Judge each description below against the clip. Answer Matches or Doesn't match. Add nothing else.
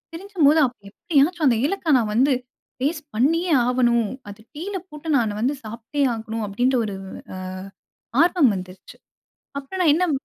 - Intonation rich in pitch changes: Matches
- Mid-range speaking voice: Doesn't match